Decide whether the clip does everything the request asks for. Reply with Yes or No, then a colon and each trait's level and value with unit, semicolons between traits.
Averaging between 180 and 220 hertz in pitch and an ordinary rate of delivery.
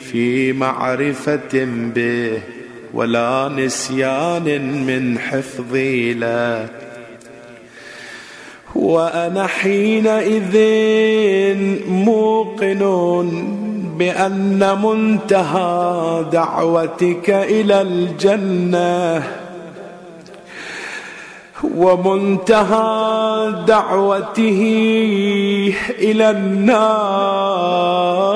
No: high, 190 Hz; slow, 40 wpm